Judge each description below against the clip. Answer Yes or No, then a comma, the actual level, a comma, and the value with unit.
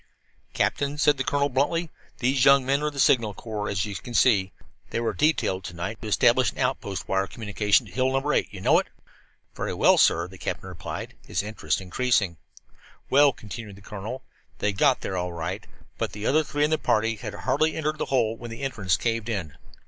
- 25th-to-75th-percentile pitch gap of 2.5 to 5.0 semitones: No, wide, 5.4 semitones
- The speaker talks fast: Yes, fast, 215 wpm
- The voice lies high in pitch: No, low, 115 Hz